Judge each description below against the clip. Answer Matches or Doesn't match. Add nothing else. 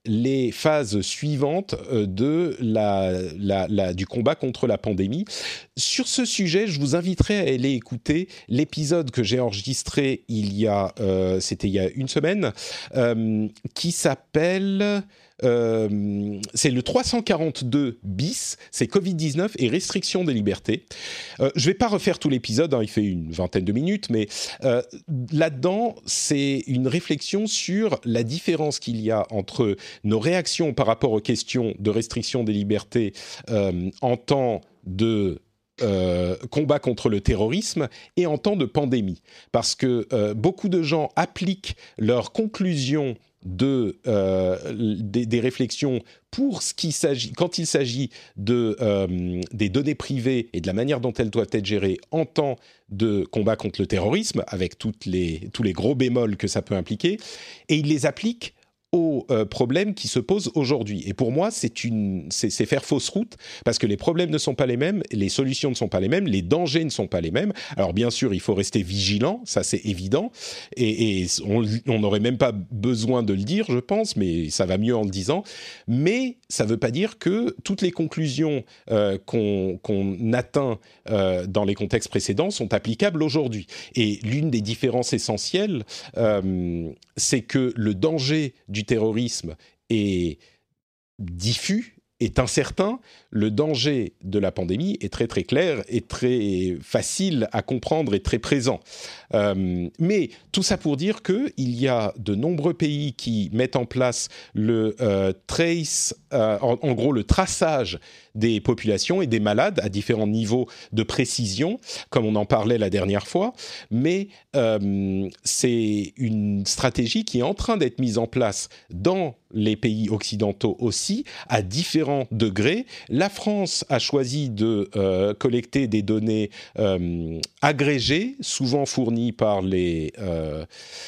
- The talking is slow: Doesn't match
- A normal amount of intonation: Doesn't match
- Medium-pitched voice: Doesn't match